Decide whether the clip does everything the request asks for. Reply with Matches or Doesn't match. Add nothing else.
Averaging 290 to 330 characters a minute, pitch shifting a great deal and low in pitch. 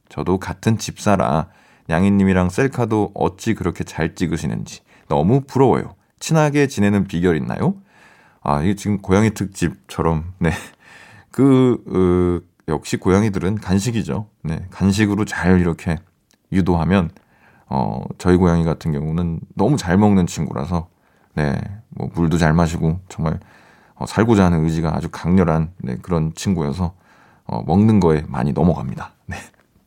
Doesn't match